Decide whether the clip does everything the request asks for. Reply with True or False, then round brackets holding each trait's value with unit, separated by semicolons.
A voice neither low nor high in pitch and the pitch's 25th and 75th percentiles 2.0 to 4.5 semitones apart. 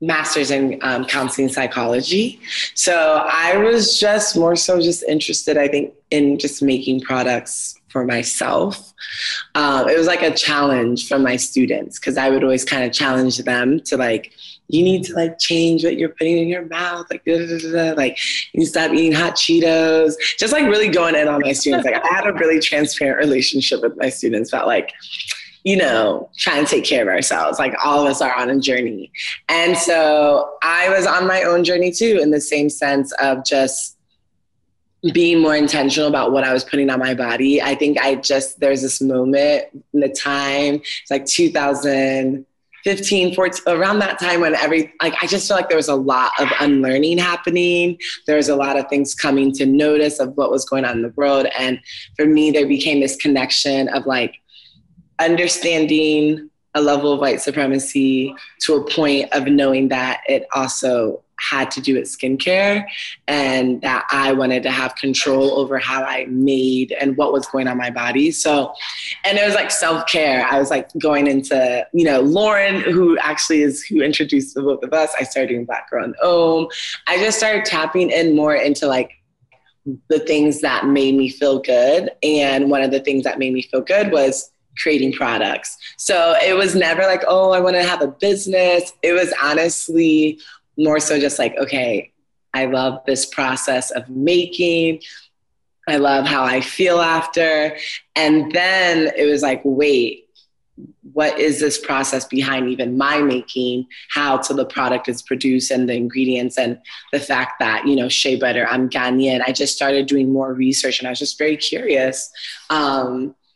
True (145 Hz; 3.7 semitones)